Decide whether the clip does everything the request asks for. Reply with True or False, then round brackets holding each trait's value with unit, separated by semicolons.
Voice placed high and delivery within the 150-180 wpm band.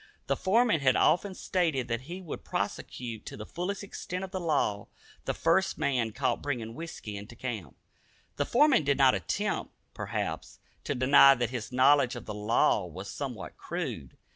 False (135 Hz; 170 wpm)